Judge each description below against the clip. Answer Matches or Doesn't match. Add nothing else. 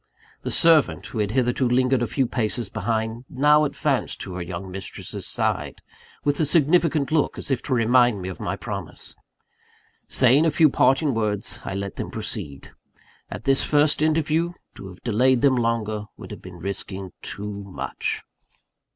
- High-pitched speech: Doesn't match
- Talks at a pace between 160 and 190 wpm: Matches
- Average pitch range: Doesn't match